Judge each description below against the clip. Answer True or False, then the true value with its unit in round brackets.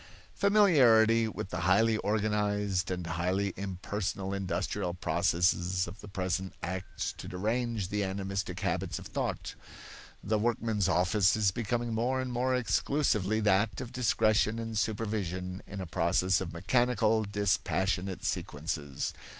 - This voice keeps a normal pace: False (130 wpm)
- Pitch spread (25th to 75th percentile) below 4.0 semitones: True (3.3 semitones)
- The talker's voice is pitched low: True (100 Hz)